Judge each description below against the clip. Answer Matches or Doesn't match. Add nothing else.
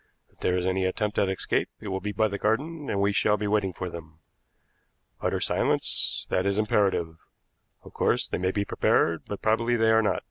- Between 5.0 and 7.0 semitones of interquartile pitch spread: Doesn't match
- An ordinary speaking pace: Doesn't match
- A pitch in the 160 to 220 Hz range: Doesn't match